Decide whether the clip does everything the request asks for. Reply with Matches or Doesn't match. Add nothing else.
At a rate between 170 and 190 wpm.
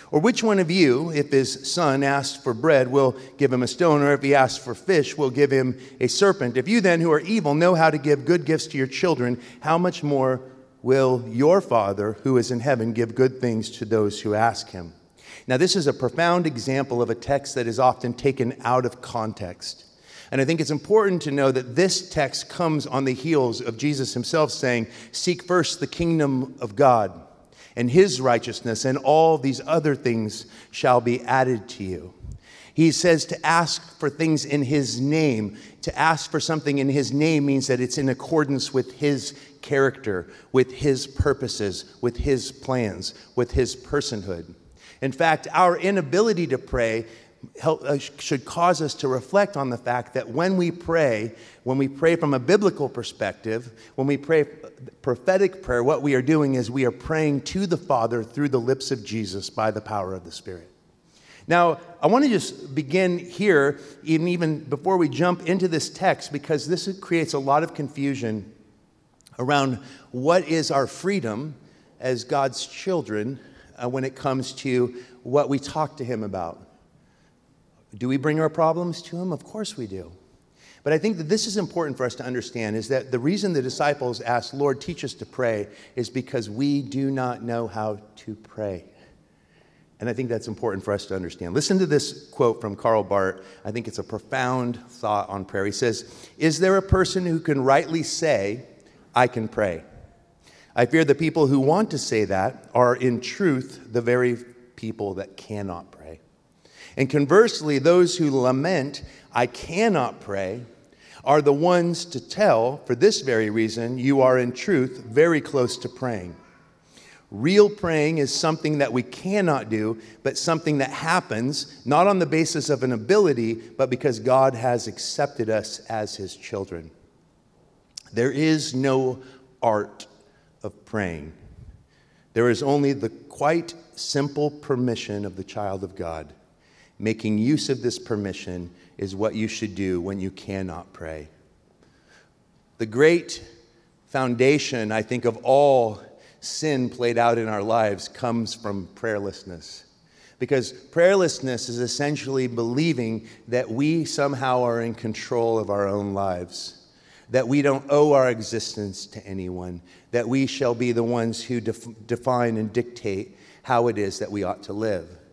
Matches